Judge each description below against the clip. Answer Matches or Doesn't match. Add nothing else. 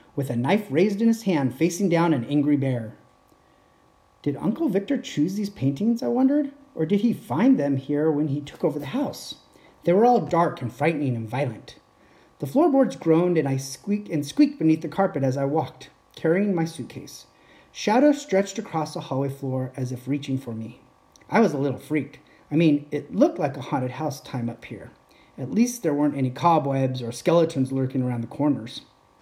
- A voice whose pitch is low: Doesn't match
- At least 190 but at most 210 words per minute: Matches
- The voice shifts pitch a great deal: Matches